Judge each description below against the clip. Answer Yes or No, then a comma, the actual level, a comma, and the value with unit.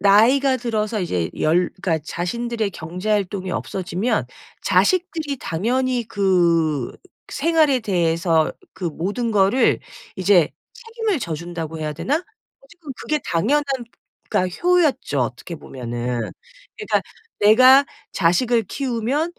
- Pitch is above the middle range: Yes, high, 205 Hz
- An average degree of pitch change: No, wide, 7.6 semitones